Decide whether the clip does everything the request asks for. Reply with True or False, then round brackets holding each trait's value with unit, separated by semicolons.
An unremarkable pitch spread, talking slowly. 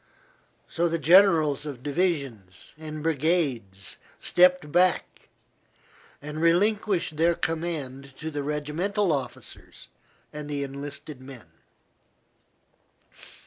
True (3.5 semitones; 95 wpm)